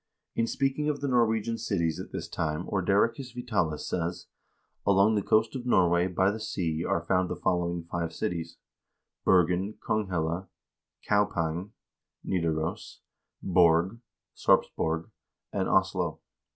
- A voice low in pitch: Yes, very low, 95 Hz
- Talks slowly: Yes, slow, 125 wpm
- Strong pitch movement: No, average, 4.3 semitones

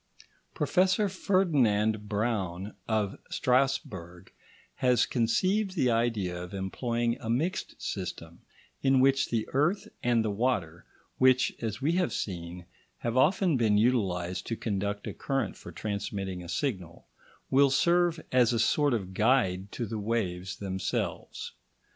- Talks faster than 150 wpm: No, slow, 135 wpm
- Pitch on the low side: Yes, low, 115 Hz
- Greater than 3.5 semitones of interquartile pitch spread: Yes, wide, 5.5 semitones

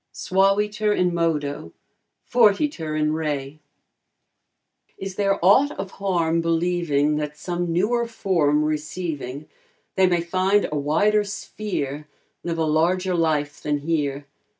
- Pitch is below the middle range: No, medium, 170 Hz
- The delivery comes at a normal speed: No, slow, 120 wpm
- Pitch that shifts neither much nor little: Yes, average, 4.4 semitones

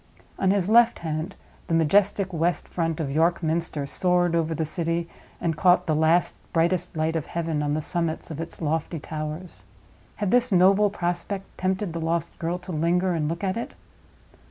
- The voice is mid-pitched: Yes, medium, 170 Hz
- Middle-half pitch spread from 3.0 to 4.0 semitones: No, narrow, 2.4 semitones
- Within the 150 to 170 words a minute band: No, average, 180 wpm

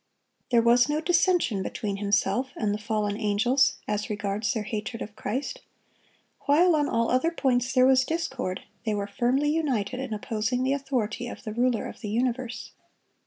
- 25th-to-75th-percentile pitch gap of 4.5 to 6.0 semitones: No, average, 4.0 semitones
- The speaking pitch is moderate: No, high, 240 Hz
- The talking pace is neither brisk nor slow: Yes, average, 170 wpm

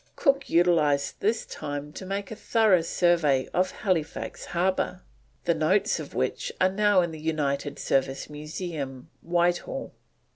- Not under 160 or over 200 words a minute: No, average, 140 wpm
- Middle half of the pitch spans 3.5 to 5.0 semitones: Yes, average, 4.2 semitones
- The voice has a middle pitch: Yes, medium, 170 Hz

